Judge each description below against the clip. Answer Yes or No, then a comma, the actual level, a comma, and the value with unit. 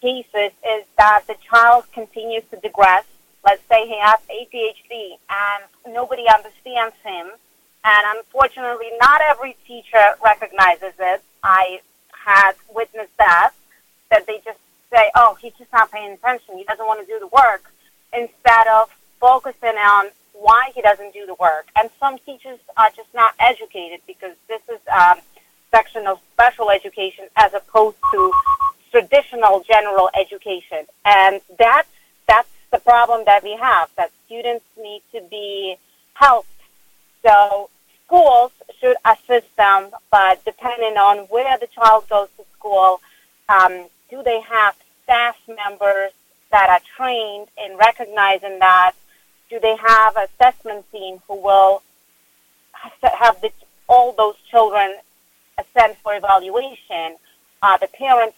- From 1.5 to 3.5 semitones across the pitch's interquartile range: Yes, average, 3.2 semitones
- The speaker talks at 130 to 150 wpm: Yes, average, 140 wpm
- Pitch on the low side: No, high, 220 Hz